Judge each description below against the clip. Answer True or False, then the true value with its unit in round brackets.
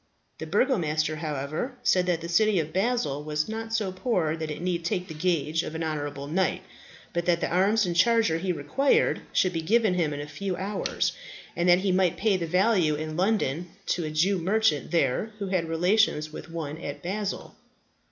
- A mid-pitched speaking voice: True (175 Hz)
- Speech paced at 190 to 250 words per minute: True (200 wpm)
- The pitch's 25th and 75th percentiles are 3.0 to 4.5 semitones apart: True (4.1 semitones)